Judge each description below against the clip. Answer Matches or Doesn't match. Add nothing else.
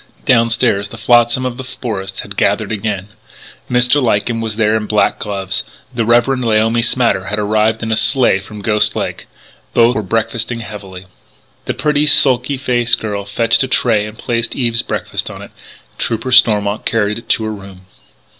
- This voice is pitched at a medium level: Doesn't match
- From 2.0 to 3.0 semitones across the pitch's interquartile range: Matches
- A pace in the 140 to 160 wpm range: Doesn't match